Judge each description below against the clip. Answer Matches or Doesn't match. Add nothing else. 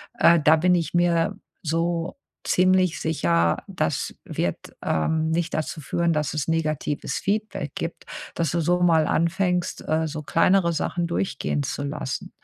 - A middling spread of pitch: Doesn't match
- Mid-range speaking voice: Matches